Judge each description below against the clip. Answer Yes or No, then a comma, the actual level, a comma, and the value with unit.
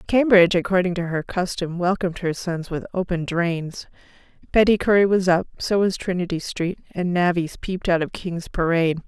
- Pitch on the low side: No, medium, 180 Hz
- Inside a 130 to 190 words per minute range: Yes, average, 165 wpm